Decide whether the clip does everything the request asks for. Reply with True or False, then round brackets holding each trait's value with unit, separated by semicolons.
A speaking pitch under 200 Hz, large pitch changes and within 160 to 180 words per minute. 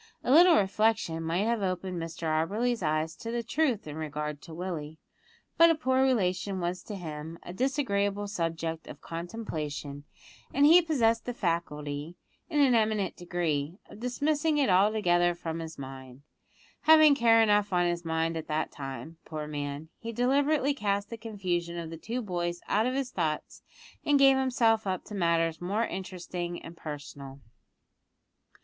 True (185 Hz; 6.1 semitones; 165 wpm)